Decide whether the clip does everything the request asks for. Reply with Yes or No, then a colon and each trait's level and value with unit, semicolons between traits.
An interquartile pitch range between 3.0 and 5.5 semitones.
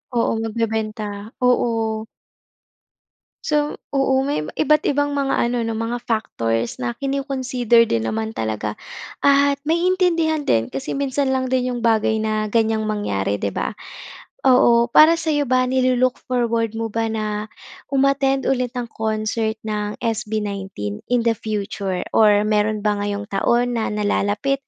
Yes: average, 4.0 semitones